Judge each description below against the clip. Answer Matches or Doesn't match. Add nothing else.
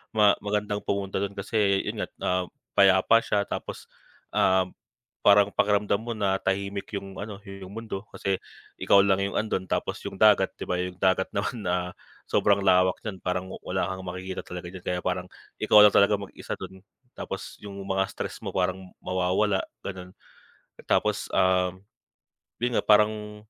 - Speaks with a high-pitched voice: Doesn't match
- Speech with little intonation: Matches